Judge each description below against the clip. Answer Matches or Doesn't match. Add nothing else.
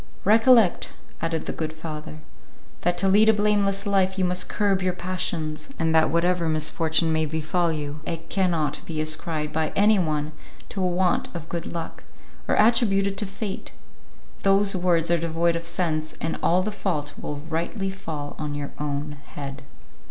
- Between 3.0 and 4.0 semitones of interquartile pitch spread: Matches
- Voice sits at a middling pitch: Matches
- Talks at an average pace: Matches